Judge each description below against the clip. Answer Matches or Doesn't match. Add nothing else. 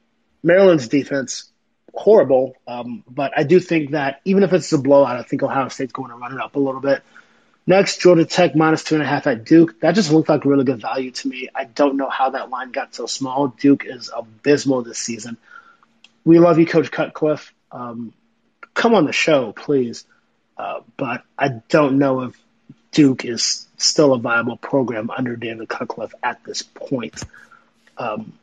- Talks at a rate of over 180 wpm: Matches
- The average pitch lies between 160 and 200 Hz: Doesn't match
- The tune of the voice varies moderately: Matches